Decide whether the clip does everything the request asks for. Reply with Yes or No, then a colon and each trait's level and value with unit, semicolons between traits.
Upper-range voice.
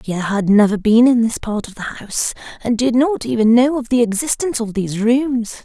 Yes: high, 230 Hz